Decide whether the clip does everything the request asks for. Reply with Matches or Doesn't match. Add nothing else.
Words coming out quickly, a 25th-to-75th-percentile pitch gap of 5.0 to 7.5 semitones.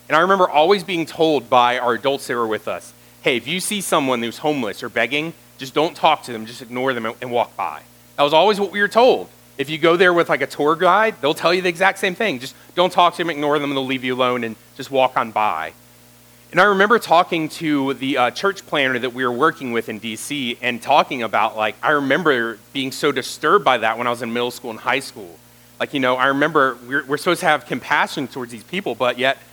Matches